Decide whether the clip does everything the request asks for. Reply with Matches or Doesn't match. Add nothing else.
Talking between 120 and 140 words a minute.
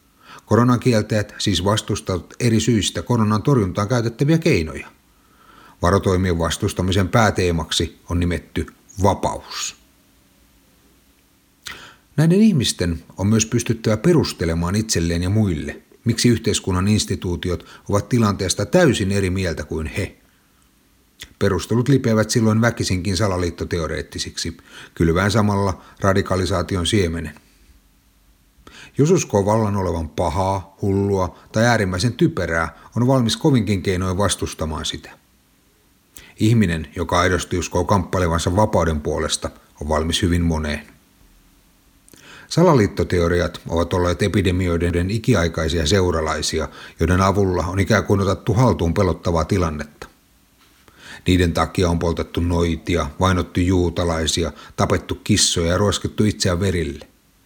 Doesn't match